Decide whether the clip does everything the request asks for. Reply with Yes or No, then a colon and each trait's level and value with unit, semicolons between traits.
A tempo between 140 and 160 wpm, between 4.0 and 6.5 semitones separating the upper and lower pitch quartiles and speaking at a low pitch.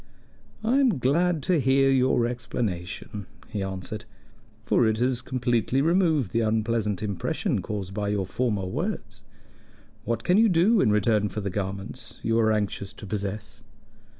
Yes: average, 150 wpm; average, 4.4 semitones; low, 110 Hz